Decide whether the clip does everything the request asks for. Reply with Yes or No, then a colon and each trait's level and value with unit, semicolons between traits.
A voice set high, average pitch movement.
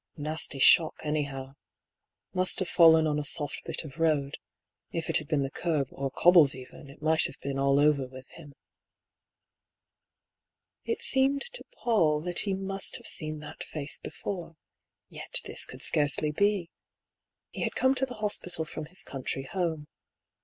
No: medium, 155 Hz; average, 4.1 semitones